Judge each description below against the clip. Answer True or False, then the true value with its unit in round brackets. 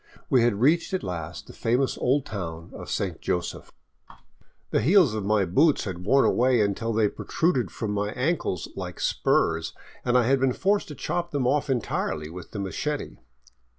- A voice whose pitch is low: True (120 Hz)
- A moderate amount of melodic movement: False (6.0 semitones)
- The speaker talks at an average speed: True (180 wpm)